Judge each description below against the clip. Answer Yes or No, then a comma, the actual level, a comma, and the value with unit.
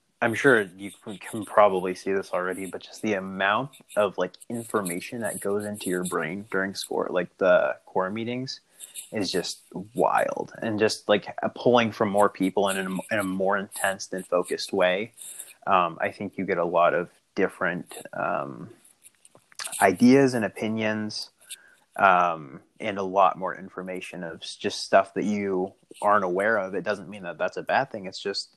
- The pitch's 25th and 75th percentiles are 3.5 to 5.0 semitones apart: No, narrow, 2.4 semitones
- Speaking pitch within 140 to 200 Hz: No, low, 100 Hz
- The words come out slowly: No, average, 170 wpm